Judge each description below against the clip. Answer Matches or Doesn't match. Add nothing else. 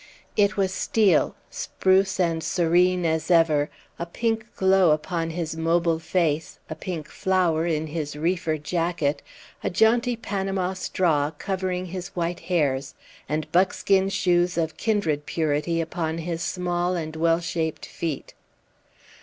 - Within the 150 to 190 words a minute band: Doesn't match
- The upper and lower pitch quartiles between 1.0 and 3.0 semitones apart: Matches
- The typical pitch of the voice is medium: Matches